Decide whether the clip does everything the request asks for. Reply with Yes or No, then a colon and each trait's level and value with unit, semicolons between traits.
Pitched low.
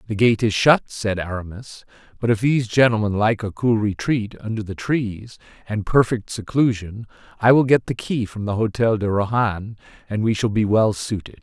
Yes: low, 110 Hz